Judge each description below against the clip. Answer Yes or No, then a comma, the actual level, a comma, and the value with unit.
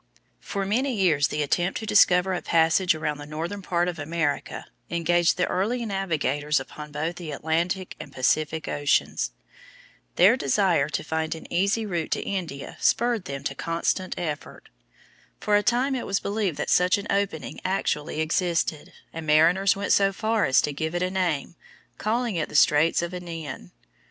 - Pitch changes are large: No, average, 4.1 semitones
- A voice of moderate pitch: Yes, medium, 175 Hz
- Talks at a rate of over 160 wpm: Yes, average, 170 wpm